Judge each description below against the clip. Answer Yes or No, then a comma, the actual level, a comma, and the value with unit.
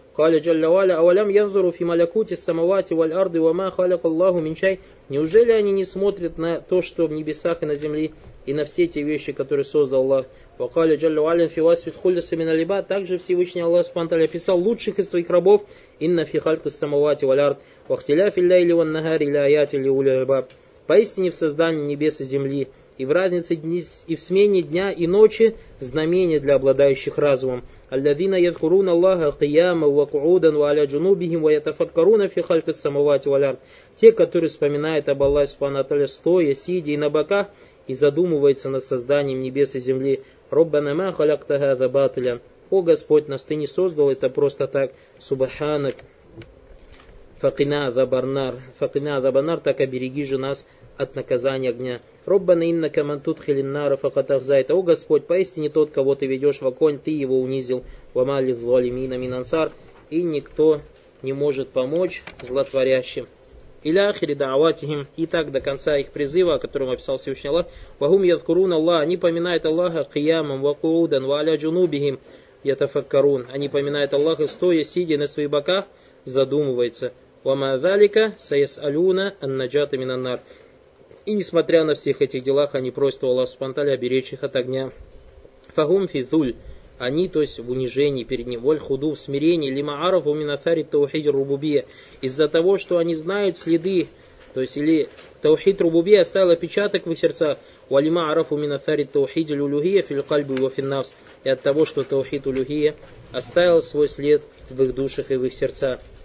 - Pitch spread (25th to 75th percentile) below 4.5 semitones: Yes, average, 4.1 semitones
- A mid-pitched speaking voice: Yes, medium, 150 Hz